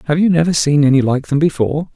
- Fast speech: Yes, fast, 245 wpm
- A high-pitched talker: No, medium, 150 Hz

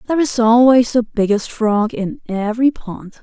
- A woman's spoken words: Yes, female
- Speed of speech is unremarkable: Yes, average, 170 wpm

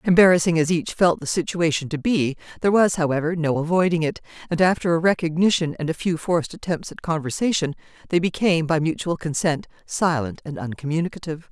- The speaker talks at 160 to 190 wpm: Yes, average, 170 wpm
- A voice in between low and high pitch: Yes, medium, 165 Hz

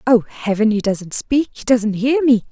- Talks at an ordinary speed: Yes, average, 190 wpm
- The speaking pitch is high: Yes, high, 230 Hz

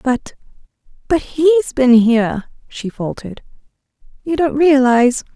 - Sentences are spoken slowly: Yes, slow, 100 wpm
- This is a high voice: Yes, very high, 265 Hz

